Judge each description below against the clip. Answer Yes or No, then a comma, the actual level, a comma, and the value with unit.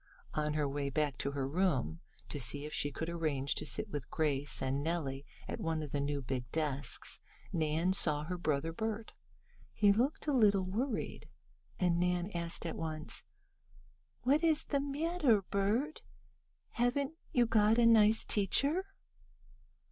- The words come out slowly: No, average, 155 wpm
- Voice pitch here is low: No, medium, 170 Hz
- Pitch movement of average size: No, wide, 7.3 semitones